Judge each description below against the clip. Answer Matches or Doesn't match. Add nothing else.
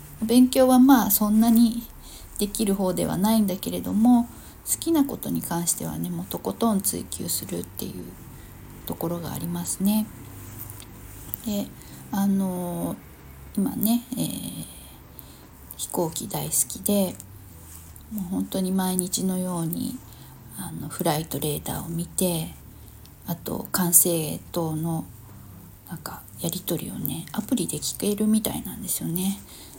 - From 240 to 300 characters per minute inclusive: Matches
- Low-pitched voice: Doesn't match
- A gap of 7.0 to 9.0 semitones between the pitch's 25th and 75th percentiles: Doesn't match